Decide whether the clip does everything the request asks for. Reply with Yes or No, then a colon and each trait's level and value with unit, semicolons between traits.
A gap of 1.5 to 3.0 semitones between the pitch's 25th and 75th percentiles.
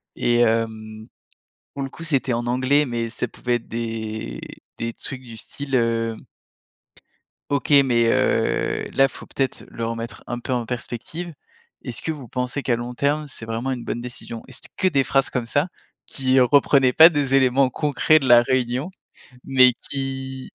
Yes: average, 2.7 semitones